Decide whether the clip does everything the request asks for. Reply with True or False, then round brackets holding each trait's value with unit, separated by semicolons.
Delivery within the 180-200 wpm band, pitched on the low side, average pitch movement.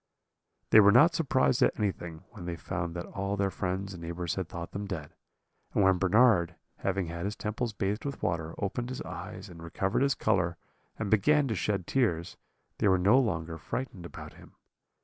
True (190 wpm; 95 Hz; 4.0 semitones)